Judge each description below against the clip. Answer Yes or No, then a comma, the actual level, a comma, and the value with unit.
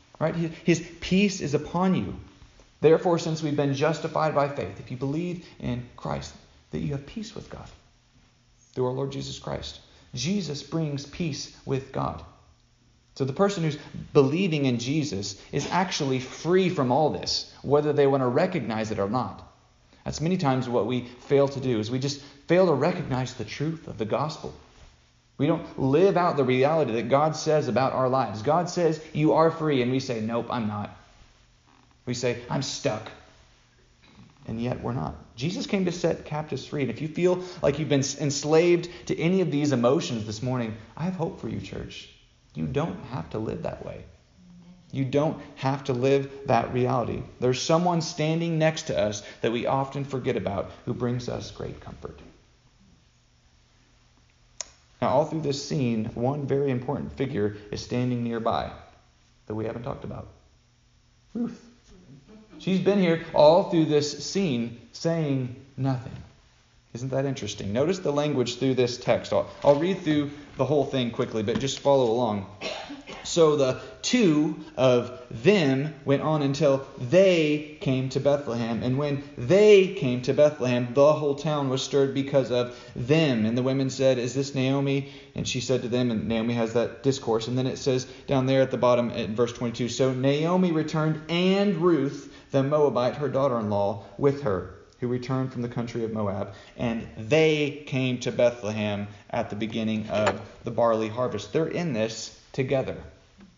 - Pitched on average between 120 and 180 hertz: Yes, low, 135 Hz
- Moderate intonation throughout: Yes, average, 4.3 semitones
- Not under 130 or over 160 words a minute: No, average, 175 wpm